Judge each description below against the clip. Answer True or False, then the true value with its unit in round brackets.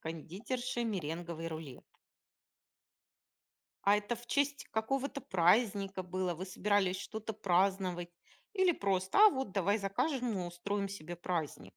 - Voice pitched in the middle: False (195 Hz)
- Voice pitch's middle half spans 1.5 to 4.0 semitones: False (4.4 semitones)